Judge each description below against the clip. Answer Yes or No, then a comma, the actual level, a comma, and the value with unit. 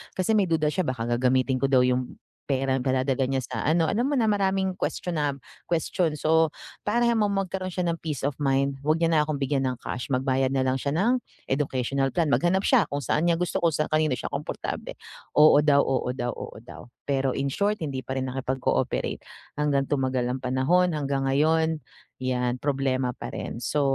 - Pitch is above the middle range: No, medium, 140 Hz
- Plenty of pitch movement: No, average, 4.0 semitones